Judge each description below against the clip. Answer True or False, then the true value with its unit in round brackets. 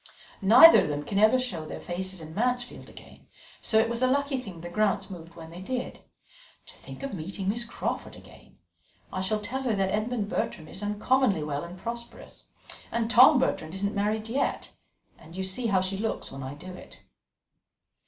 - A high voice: True (205 Hz)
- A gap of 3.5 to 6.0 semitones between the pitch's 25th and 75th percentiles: True (4.7 semitones)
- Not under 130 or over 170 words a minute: False (195 wpm)